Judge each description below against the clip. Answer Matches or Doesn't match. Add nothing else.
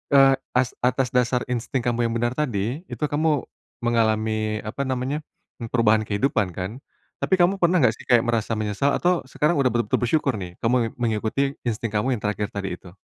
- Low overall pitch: Matches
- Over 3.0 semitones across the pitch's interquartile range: Matches